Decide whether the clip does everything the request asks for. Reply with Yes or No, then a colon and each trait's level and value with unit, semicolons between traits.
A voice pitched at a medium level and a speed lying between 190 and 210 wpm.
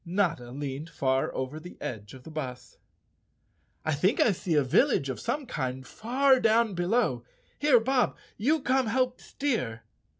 No: medium, 175 Hz; average, 160 wpm